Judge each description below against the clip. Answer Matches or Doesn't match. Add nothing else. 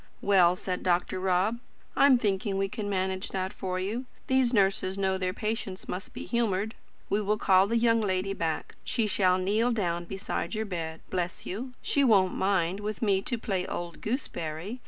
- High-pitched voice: Matches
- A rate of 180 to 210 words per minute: Matches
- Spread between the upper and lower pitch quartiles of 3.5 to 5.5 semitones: Doesn't match